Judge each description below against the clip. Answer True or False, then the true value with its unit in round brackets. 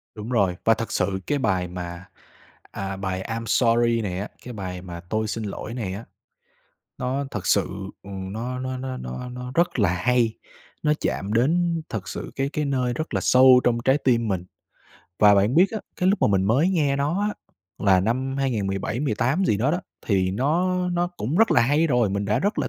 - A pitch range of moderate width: False (5.7 semitones)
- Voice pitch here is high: False (115 Hz)